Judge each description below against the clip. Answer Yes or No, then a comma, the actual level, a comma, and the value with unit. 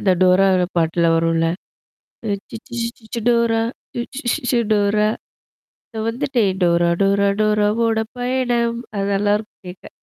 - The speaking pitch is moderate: No, high, 215 Hz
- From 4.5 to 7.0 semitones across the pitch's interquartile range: No, average, 3.2 semitones